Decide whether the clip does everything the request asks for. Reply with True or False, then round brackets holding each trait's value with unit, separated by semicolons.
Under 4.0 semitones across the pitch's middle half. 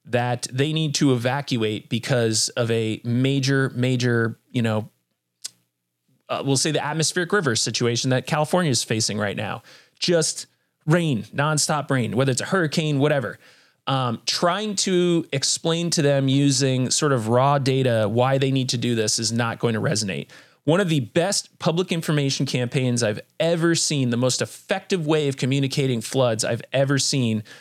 False (4.3 semitones)